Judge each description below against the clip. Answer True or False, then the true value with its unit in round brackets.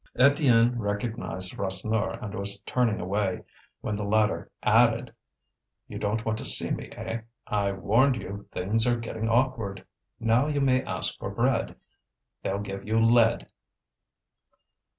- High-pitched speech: False (110 Hz)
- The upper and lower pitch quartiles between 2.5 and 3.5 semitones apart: True (2.8 semitones)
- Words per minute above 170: False (140 wpm)